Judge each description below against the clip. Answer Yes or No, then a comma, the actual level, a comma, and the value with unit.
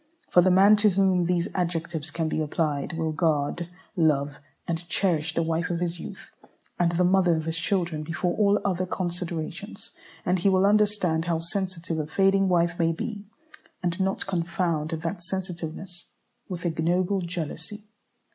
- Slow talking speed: No, average, 160 wpm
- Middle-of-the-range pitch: Yes, medium, 175 Hz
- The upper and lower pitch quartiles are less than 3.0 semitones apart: Yes, narrow, 2.4 semitones